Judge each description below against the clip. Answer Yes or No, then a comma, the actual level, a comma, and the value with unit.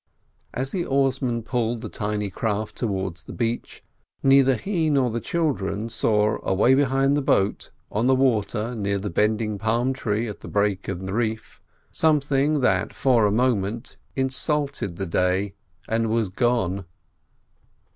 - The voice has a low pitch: Yes, low, 115 Hz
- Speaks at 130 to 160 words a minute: Yes, average, 150 wpm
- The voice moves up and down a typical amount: Yes, average, 4.4 semitones